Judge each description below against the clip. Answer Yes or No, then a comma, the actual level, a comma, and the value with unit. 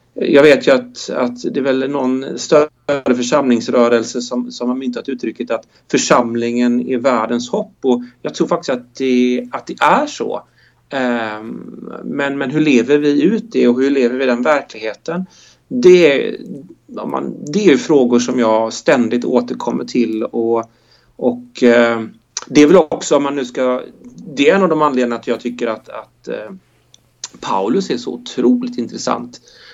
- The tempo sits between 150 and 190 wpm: Yes, average, 165 wpm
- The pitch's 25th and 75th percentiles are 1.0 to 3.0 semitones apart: Yes, average, 2.7 semitones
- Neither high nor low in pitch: No, low, 125 Hz